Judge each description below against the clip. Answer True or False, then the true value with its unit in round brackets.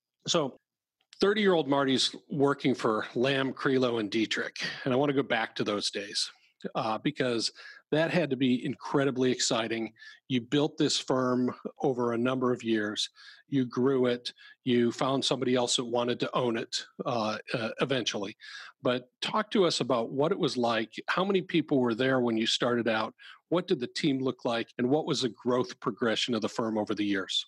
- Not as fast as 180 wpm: False (190 wpm)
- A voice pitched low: True (125 Hz)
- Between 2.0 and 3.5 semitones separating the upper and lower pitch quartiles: True (2.7 semitones)